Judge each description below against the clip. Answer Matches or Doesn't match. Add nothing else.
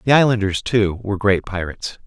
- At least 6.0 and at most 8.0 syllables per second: Matches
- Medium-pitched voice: Doesn't match